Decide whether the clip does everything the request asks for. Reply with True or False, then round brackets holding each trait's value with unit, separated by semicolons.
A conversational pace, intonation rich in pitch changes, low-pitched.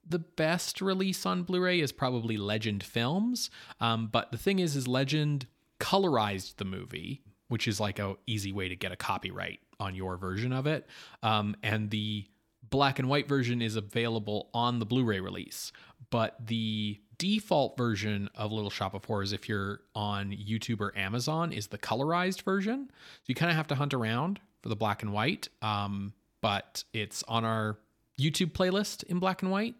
True (180 wpm; 6.6 semitones; 115 Hz)